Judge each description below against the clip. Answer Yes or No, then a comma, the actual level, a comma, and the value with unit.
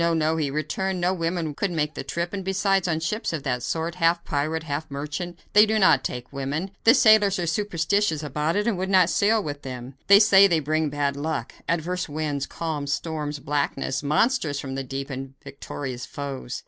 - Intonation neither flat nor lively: Yes, average, 4.5 semitones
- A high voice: No, medium, 160 Hz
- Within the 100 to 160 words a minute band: No, average, 200 wpm